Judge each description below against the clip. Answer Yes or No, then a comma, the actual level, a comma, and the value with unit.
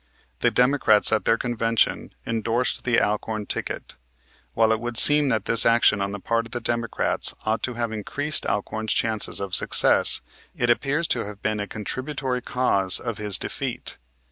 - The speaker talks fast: No, average, 170 wpm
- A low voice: Yes, low, 115 Hz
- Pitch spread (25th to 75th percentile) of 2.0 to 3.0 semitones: Yes, narrow, 2.4 semitones